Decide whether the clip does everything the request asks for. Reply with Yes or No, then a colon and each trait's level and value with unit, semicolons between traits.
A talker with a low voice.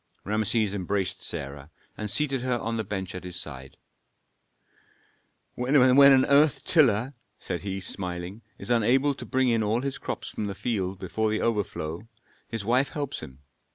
Yes: low, 110 Hz